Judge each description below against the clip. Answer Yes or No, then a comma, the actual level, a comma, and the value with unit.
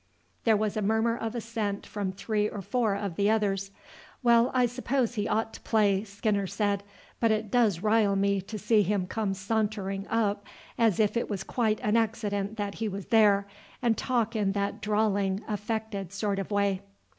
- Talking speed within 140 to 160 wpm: No, average, 185 wpm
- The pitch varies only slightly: Yes, narrow, 1.9 semitones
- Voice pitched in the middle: No, high, 210 Hz